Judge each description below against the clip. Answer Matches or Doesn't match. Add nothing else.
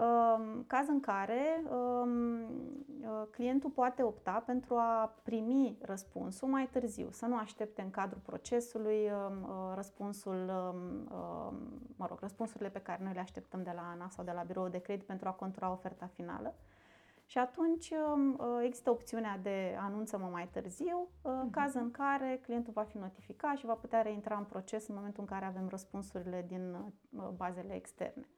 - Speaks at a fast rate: Doesn't match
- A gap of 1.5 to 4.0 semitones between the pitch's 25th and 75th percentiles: Doesn't match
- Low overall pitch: Doesn't match